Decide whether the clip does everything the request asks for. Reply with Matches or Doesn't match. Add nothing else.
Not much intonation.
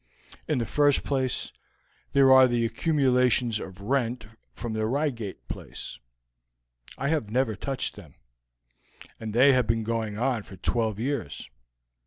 Doesn't match